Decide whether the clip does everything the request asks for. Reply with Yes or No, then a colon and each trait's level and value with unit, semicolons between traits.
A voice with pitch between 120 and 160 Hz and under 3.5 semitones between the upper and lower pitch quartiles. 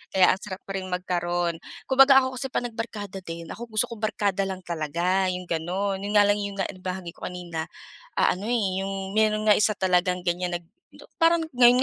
No: high, 190 Hz; average, 2.9 semitones